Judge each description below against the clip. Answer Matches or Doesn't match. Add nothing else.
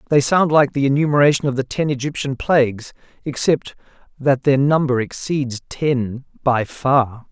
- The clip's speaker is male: Matches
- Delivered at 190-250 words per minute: Doesn't match